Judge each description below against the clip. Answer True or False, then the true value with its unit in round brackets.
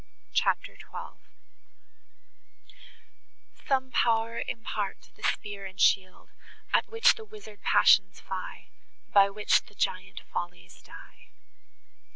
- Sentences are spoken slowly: True (105 wpm)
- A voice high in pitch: True (205 Hz)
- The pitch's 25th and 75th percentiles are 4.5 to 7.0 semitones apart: False (3.4 semitones)